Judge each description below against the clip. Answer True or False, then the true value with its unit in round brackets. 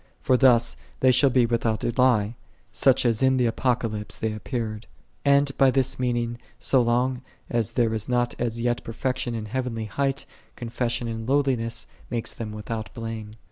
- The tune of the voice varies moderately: False (2.1 semitones)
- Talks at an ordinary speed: True (180 wpm)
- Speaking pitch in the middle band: False (120 Hz)